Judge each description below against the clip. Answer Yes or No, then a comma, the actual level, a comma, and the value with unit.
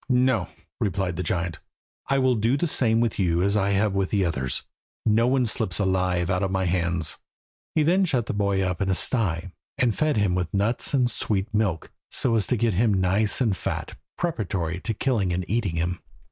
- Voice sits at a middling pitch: No, low, 100 Hz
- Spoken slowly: No, average, 200 wpm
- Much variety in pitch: No, average, 4.3 semitones